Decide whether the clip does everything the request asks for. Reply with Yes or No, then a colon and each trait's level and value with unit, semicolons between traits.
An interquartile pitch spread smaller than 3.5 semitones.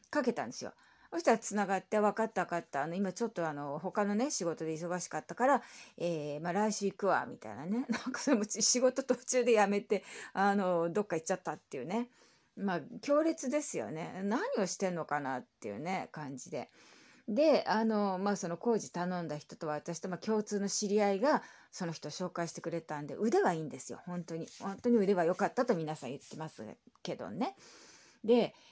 No: average, 5.3 semitones